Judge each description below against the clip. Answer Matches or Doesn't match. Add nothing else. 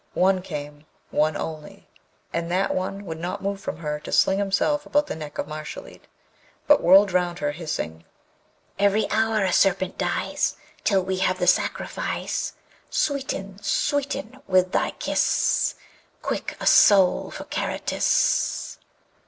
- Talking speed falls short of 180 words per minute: Matches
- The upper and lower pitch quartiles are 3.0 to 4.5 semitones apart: Matches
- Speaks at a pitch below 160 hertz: Doesn't match